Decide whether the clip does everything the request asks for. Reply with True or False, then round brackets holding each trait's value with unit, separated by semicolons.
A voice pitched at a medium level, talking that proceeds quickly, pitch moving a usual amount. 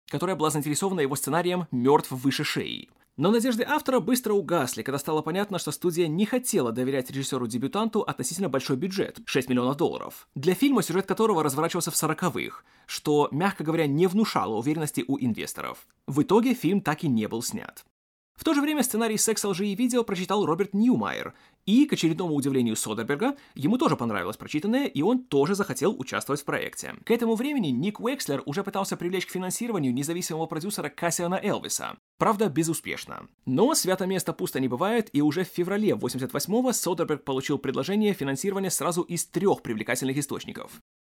False (175 Hz; 170 wpm; 6.4 semitones)